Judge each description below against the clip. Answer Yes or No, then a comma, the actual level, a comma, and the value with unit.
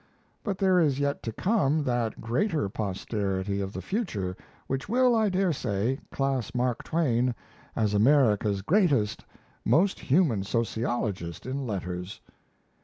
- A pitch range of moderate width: No, wide, 7.5 semitones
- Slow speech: Yes, slow, 130 wpm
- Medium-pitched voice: No, low, 125 Hz